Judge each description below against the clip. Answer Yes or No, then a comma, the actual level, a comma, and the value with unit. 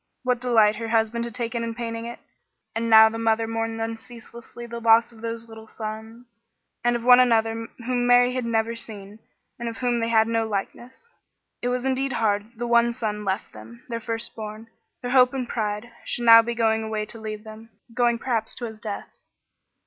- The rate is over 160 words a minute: Yes, average, 200 wpm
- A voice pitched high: Yes, high, 230 Hz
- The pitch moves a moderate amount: No, narrow, 1.3 semitones